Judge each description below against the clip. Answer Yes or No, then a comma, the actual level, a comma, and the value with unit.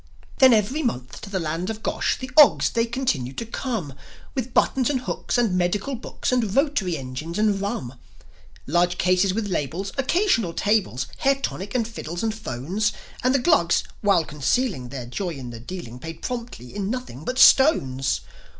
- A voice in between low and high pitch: No, high, 200 Hz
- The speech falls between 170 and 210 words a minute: Yes, average, 180 wpm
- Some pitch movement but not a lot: No, wide, 7.7 semitones